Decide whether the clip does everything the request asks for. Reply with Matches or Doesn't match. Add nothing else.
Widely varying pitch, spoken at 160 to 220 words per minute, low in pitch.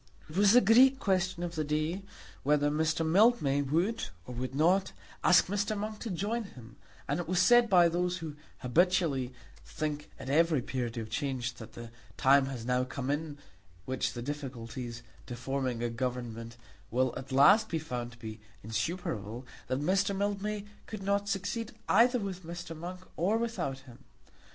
Doesn't match